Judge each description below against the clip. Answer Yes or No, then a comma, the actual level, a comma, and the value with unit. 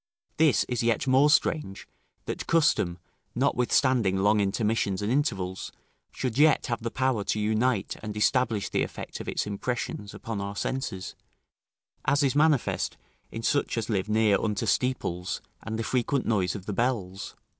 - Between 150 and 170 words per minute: Yes, average, 155 wpm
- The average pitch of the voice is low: Yes, low, 115 Hz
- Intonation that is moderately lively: Yes, average, 4.3 semitones